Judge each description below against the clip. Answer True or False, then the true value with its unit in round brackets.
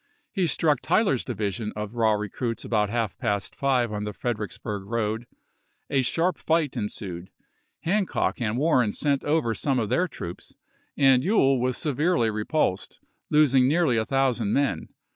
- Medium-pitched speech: False (125 Hz)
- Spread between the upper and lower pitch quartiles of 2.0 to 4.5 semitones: False (5.5 semitones)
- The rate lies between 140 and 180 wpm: True (160 wpm)